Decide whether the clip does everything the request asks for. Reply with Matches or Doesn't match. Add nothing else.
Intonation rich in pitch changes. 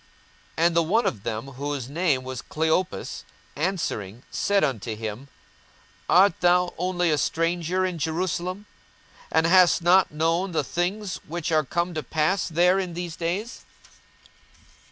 Doesn't match